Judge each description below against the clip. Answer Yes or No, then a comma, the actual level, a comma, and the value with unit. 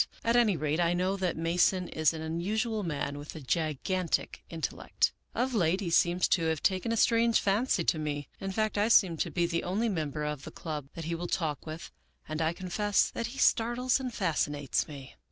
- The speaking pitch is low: No, medium, 175 Hz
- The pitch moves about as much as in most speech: Yes, average, 4.8 semitones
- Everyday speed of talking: No, fast, 210 wpm